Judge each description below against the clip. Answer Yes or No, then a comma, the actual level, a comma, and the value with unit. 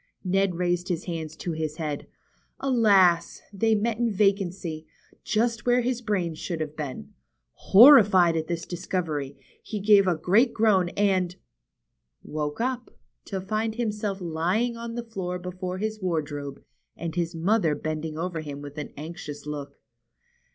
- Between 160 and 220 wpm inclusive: No, average, 150 wpm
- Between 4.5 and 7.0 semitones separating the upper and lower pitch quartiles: Yes, average, 5.1 semitones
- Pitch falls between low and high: Yes, medium, 180 Hz